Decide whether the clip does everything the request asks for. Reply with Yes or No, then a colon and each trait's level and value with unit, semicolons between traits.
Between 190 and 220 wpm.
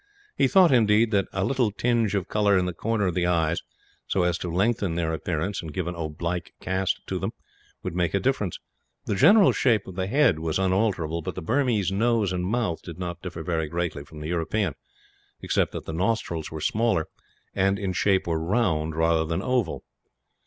Yes: average, 200 wpm